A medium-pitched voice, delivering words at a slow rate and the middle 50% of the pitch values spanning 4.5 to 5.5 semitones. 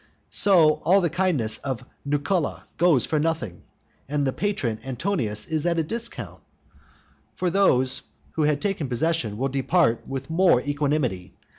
No: medium, 150 Hz; average, 145 wpm; average, 5.1 semitones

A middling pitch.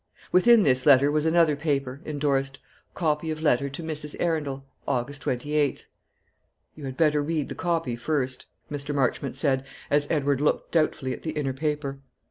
Yes: medium, 145 Hz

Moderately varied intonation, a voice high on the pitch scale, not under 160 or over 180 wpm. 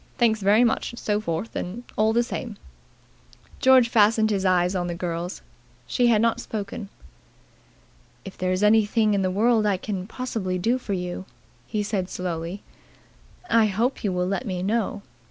Yes: average, 3.5 semitones; high, 205 Hz; average, 170 wpm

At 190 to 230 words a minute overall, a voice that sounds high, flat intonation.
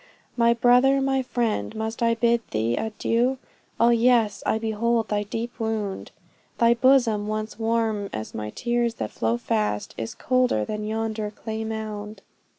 No: average, 155 wpm; high, 220 Hz; narrow, 2.1 semitones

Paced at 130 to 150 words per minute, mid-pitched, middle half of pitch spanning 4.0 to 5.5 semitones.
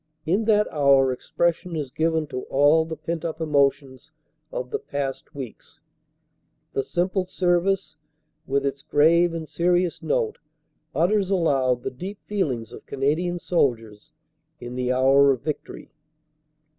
Yes: slow, 135 wpm; medium, 155 Hz; average, 4.6 semitones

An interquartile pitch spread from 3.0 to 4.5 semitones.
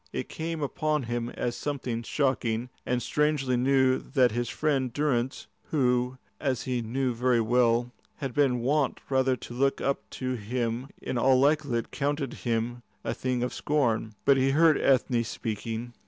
No: narrow, 2.4 semitones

